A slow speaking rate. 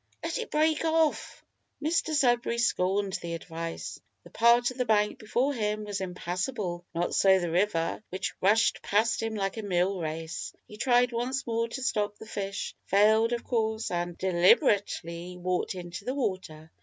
No: average, 170 wpm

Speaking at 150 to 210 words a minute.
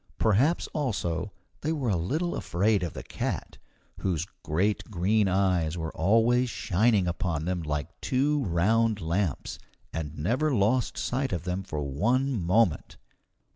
No: average, 140 wpm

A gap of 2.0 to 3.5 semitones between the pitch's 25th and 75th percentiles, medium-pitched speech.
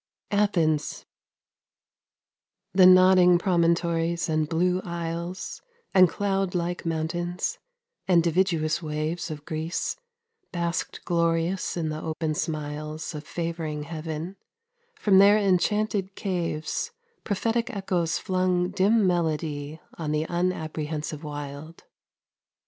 Yes: average, 2.8 semitones; medium, 170 Hz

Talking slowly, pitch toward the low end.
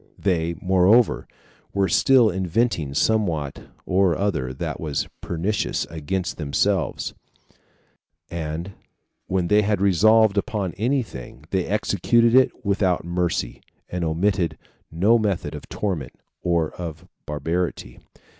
Yes: slow, 115 wpm; very low, 90 Hz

